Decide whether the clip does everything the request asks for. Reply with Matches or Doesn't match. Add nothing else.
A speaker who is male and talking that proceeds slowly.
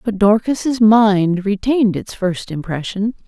Doesn't match